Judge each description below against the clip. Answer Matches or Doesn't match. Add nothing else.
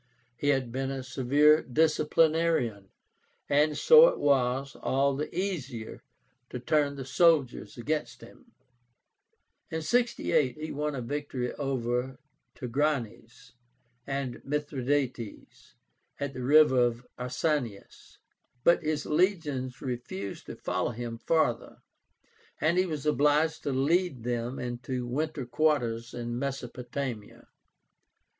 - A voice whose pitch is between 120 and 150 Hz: Matches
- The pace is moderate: Doesn't match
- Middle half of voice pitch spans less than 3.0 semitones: Doesn't match